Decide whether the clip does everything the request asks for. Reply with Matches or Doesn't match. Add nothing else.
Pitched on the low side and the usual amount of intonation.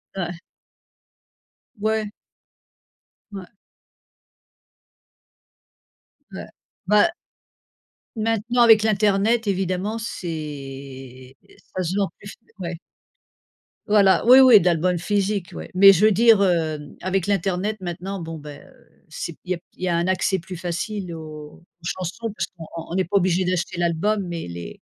Doesn't match